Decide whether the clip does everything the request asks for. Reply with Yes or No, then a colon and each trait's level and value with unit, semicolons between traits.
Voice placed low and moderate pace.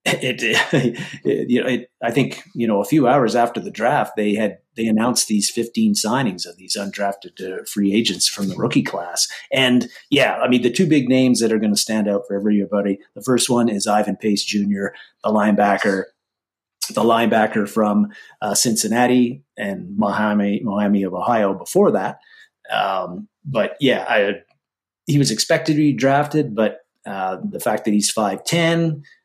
Yes: low, 110 Hz; average, 180 wpm